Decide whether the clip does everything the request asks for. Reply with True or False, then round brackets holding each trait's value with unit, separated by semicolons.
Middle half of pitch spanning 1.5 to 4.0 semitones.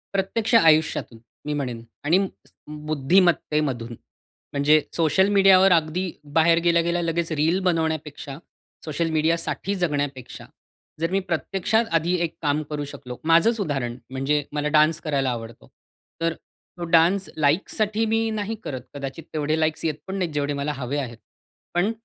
True (3.5 semitones)